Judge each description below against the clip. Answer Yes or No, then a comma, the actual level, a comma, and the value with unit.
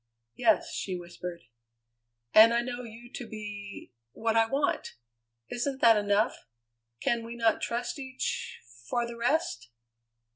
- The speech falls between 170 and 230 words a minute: No, slow, 135 wpm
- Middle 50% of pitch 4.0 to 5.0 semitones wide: No, average, 2.9 semitones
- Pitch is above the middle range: Yes, high, 230 Hz